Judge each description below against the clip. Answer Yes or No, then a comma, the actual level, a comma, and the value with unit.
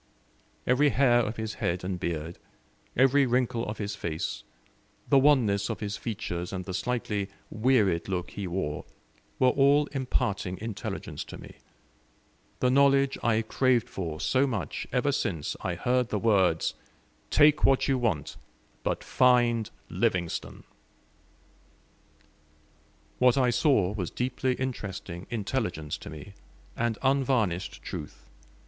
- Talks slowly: Yes, slow, 130 wpm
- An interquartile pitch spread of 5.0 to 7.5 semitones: Yes, wide, 5.6 semitones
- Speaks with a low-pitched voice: Yes, low, 110 Hz